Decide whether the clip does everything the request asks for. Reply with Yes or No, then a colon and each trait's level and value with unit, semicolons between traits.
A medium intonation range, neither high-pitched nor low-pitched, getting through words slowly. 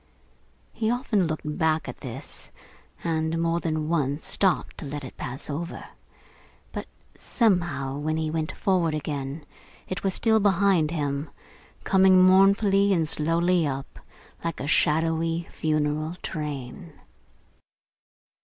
Yes: average, 3.5 semitones; medium, 160 Hz; slow, 125 wpm